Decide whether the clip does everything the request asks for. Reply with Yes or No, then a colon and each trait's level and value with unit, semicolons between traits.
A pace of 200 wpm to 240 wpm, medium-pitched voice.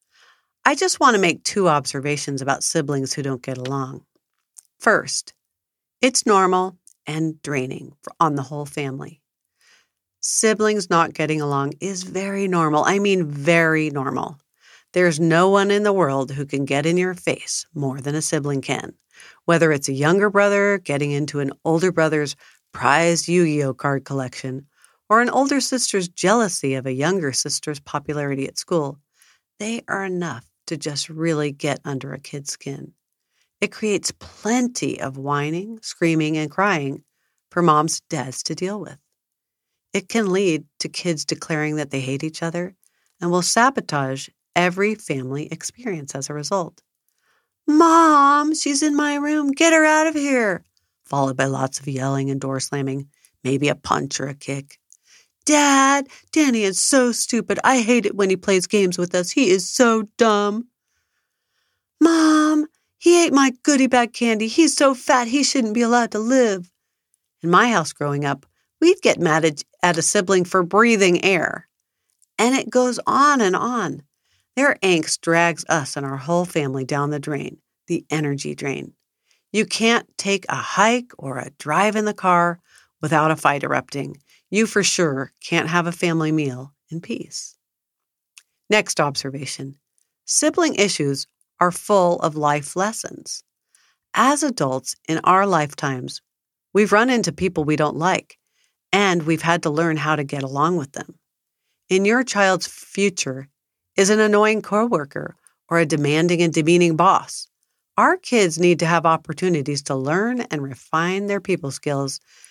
No: average, 160 wpm; medium, 170 Hz